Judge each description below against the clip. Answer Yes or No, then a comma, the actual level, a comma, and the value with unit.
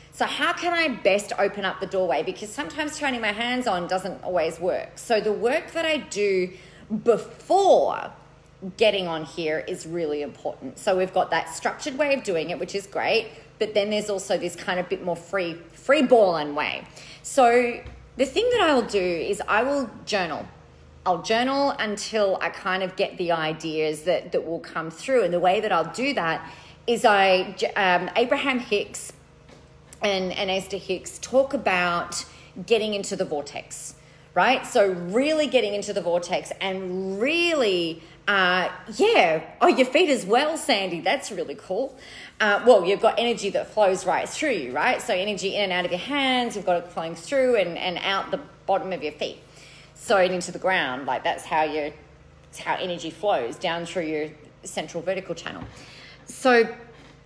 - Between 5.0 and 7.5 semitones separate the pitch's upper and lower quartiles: Yes, wide, 5.4 semitones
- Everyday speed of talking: Yes, average, 180 wpm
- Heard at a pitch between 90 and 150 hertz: No, high, 190 Hz